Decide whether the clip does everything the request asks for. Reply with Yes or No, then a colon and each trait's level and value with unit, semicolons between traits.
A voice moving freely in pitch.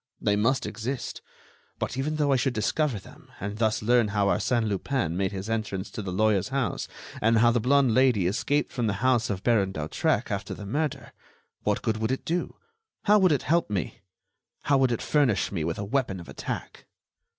No: average, 4.7 semitones